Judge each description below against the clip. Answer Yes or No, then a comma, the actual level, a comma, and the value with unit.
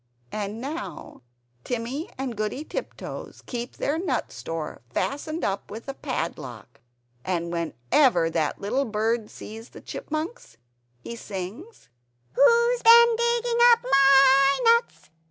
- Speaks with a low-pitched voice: No, very high, 255 Hz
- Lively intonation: Yes, wide, 8.2 semitones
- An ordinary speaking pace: No, slow, 125 wpm